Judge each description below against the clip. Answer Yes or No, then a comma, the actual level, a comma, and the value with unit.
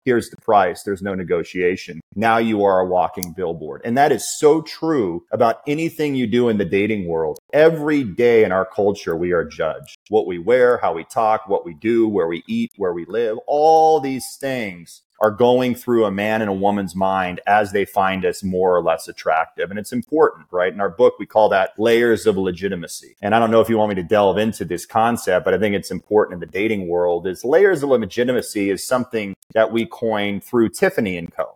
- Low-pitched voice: Yes, low, 110 Hz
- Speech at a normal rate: No, fast, 220 wpm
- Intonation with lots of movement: Yes, wide, 7.4 semitones